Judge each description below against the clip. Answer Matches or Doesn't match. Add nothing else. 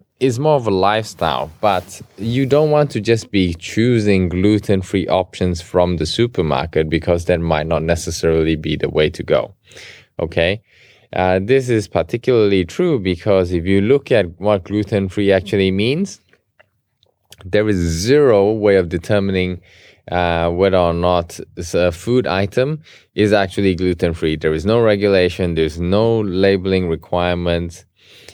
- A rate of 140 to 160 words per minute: Matches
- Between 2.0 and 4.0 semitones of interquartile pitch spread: Matches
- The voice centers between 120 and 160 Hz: Doesn't match